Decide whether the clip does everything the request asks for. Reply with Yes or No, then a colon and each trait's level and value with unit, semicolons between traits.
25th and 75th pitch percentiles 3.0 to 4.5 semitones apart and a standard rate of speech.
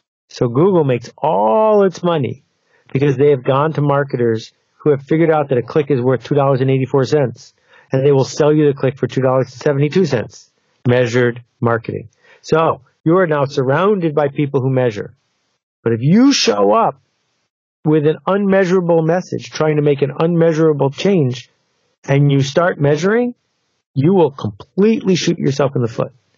Yes: average, 4.2 semitones; average, 155 wpm